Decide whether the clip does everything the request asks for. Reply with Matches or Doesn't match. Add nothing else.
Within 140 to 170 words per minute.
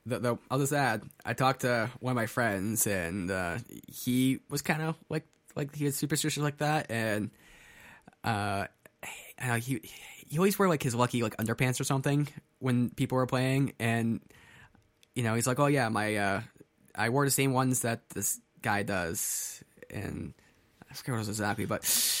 Doesn't match